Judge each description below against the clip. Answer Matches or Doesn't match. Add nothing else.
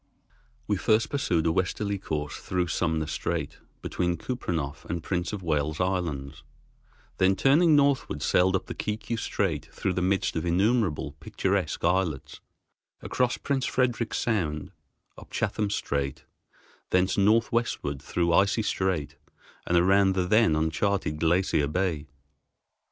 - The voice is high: Doesn't match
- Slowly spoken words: Matches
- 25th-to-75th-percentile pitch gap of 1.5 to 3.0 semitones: Doesn't match